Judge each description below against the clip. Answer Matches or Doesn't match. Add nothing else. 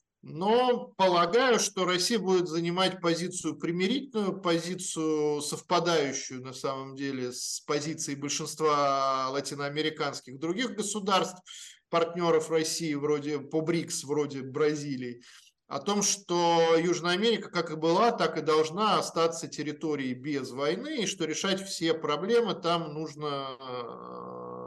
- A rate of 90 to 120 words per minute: Matches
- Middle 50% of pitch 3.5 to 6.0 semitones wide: Matches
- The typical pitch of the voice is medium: Matches